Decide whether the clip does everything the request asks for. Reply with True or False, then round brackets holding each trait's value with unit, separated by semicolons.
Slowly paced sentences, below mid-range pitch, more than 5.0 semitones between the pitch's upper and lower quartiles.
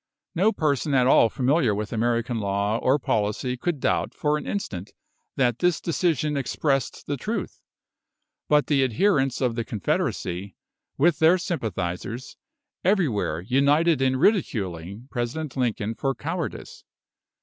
True (130 wpm; 130 Hz; 5.6 semitones)